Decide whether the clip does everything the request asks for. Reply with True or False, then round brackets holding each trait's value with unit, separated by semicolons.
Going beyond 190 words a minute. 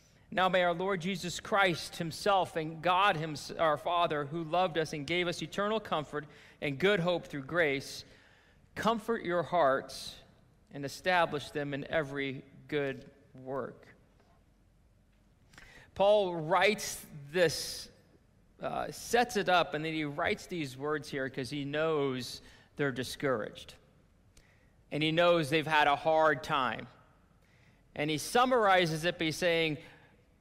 False (135 wpm)